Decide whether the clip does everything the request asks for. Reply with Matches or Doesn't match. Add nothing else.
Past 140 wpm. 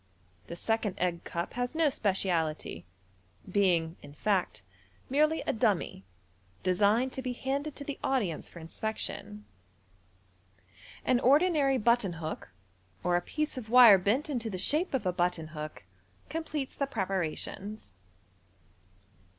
Doesn't match